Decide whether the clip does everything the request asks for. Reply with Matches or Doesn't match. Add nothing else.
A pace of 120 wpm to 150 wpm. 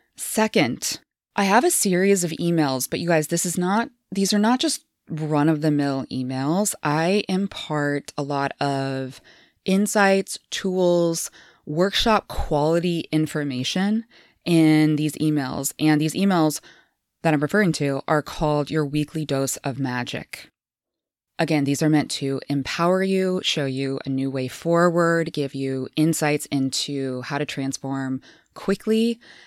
Matches